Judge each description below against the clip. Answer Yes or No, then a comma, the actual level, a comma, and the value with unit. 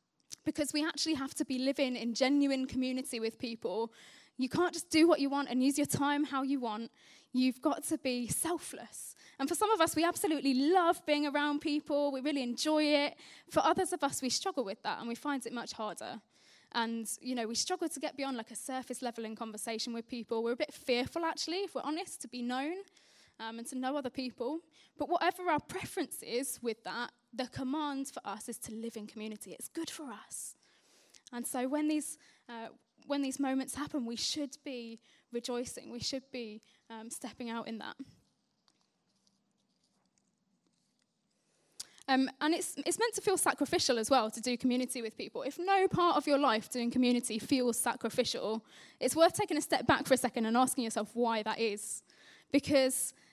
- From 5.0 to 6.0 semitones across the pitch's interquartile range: No, average, 4.2 semitones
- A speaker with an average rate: Yes, average, 195 wpm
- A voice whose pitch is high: Yes, very high, 265 Hz